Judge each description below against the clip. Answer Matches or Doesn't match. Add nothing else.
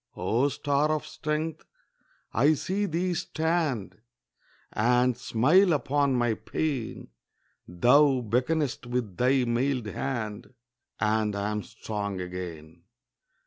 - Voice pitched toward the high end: Doesn't match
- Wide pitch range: Matches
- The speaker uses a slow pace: Matches